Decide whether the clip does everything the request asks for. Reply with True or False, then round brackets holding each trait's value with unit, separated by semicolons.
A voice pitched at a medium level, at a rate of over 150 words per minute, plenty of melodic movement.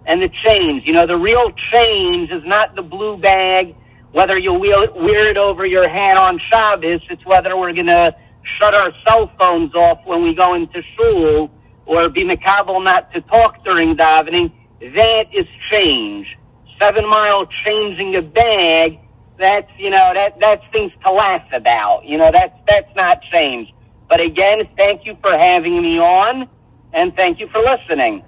False (200 Hz; 170 wpm; 9.0 semitones)